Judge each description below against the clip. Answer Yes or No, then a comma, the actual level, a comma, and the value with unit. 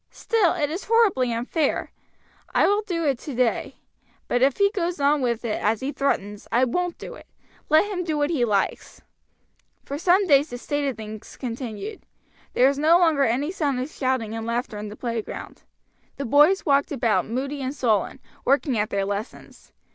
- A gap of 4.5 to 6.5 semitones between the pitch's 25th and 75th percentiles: Yes, wide, 5.5 semitones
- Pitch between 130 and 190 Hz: No, very high, 275 Hz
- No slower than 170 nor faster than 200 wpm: Yes, average, 185 wpm